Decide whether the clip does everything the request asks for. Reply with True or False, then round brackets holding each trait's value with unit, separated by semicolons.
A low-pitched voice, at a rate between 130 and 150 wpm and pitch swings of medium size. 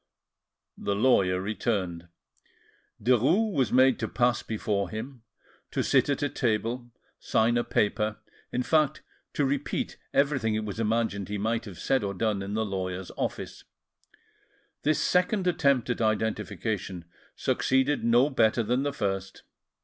True (115 Hz; 140 wpm; 4.5 semitones)